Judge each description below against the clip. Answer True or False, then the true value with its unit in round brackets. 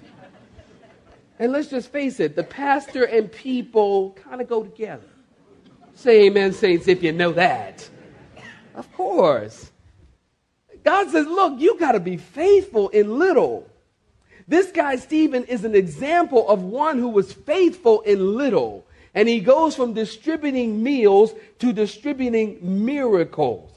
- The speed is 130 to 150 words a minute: True (135 wpm)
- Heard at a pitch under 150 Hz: False (245 Hz)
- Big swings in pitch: True (6.9 semitones)